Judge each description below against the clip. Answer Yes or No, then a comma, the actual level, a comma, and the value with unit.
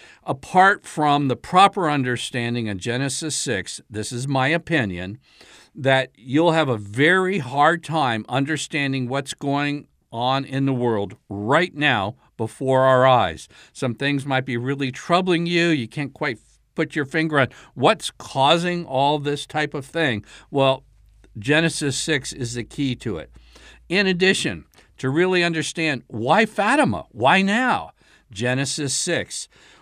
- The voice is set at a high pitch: No, medium, 140 Hz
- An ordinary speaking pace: Yes, average, 145 wpm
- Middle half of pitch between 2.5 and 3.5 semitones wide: No, average, 4.5 semitones